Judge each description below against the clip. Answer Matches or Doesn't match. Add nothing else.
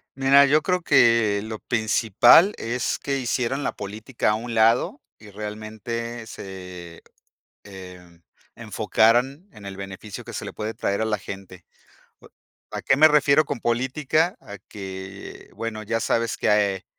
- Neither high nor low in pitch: Doesn't match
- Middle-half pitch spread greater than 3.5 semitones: Matches